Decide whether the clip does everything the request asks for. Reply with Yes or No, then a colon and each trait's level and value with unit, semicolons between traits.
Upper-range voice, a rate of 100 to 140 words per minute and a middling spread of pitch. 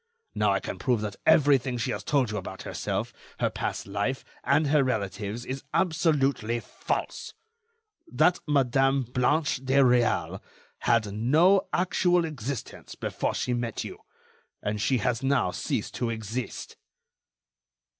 No: low, 130 Hz; slow, 135 wpm; average, 4.3 semitones